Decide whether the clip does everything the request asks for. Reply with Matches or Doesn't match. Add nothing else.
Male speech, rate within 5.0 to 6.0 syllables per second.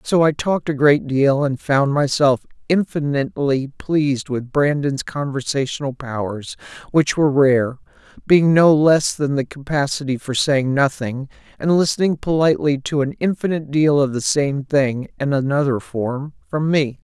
Doesn't match